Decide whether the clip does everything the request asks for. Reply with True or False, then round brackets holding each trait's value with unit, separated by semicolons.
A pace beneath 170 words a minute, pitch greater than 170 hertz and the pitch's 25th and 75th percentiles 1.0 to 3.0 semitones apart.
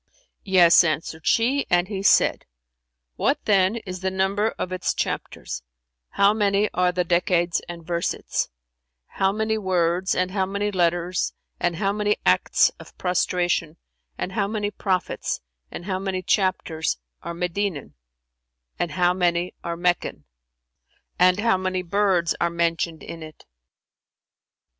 True (140 wpm; 185 Hz; 2.5 semitones)